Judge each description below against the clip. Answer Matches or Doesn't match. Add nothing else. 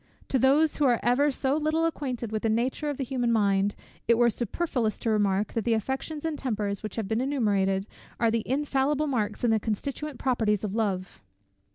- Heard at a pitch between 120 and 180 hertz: Doesn't match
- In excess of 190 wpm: Matches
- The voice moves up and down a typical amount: Matches